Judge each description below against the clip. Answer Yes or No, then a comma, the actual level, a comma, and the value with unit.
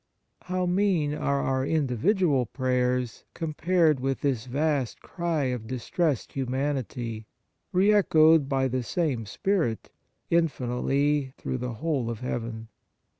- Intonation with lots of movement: No, average, 4.4 semitones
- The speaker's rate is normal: No, slow, 125 wpm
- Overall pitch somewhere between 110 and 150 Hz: Yes, low, 135 Hz